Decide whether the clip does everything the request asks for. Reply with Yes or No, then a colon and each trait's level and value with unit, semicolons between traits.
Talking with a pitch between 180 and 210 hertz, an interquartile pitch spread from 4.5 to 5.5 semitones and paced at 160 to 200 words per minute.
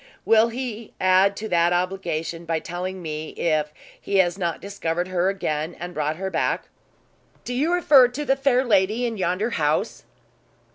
Yes: medium, 185 Hz; average, 5.1 semitones; average, 170 wpm